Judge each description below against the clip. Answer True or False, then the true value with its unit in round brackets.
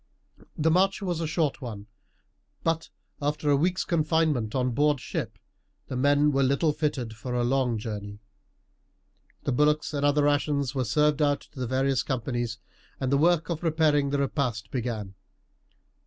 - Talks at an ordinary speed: True (160 wpm)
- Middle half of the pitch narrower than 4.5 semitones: True (3.3 semitones)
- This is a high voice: False (140 Hz)